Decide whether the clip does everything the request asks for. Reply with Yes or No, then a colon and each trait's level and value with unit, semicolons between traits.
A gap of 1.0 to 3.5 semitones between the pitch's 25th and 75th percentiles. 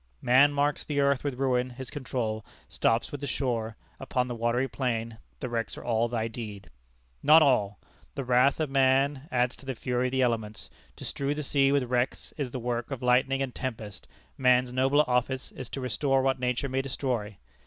Yes: narrow, 2.4 semitones